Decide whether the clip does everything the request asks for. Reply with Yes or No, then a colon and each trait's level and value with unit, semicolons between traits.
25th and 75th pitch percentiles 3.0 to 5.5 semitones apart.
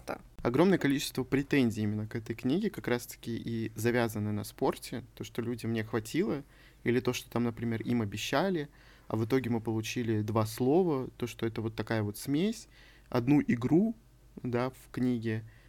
No: narrow, 2.5 semitones